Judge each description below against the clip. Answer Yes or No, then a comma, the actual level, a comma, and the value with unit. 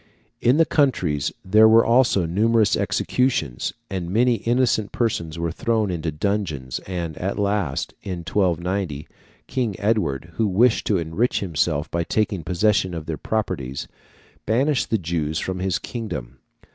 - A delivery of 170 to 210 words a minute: No, average, 145 wpm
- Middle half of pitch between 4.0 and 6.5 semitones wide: Yes, average, 5.2 semitones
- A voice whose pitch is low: Yes, very low, 95 Hz